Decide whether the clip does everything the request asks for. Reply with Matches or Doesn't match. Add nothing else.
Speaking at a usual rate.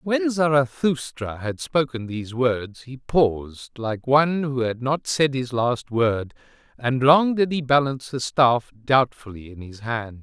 Matches